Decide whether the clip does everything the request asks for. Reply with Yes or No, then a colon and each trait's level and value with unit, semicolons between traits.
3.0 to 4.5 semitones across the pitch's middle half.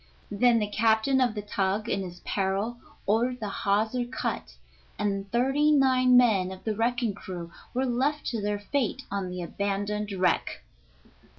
Yes: average, 3.8 semitones